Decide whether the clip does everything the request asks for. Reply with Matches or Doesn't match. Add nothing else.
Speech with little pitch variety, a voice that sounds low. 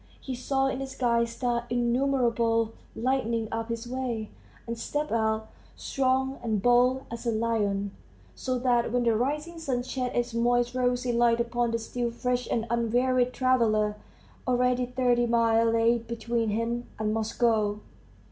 Doesn't match